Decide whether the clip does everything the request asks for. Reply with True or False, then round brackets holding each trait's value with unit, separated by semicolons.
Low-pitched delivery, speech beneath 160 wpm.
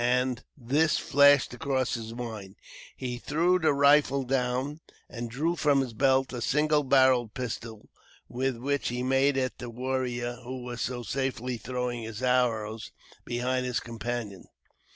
True (125 Hz; 150 wpm)